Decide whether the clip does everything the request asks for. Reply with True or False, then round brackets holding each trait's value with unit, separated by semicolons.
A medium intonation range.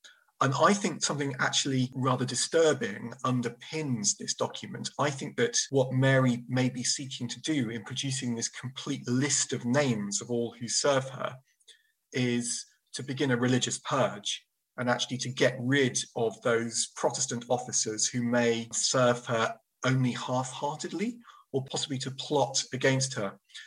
False (2.1 semitones)